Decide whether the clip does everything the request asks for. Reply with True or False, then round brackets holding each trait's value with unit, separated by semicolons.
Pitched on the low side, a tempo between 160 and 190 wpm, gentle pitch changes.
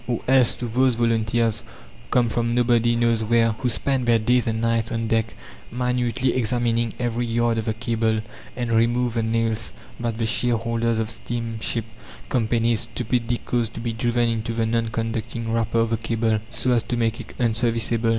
True (115 Hz; 180 wpm; 1.0 semitones)